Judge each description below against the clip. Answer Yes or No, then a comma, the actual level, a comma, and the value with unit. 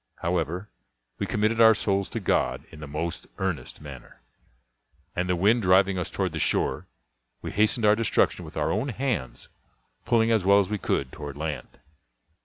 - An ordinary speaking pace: Yes, average, 175 wpm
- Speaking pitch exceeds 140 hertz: No, very low, 95 Hz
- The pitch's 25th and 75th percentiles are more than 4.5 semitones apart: Yes, average, 4.9 semitones